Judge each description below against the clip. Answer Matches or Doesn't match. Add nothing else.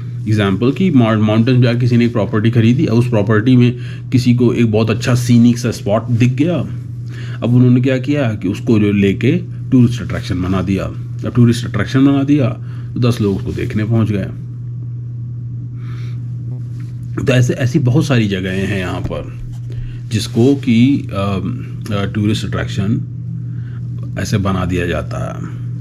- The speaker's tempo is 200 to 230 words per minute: Doesn't match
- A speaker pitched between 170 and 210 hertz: Doesn't match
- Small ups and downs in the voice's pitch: Matches